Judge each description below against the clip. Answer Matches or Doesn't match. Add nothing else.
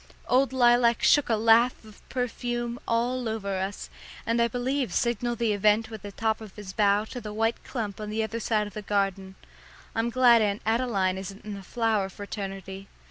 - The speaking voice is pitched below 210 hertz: Doesn't match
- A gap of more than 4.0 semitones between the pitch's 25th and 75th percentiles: Doesn't match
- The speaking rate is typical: Matches